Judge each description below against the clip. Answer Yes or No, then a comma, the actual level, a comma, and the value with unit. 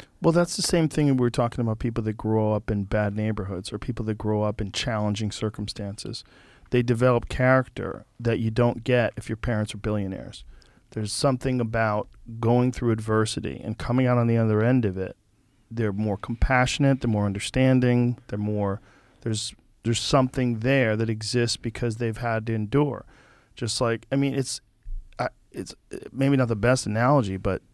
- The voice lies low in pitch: Yes, low, 115 Hz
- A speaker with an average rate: Yes, average, 180 wpm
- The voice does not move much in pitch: No, average, 3.0 semitones